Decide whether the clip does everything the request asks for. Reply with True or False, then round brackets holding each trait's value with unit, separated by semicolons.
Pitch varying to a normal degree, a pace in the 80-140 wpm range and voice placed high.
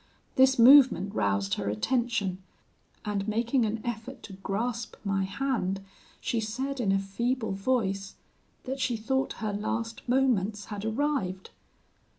True (4.3 semitones; 135 wpm; 220 Hz)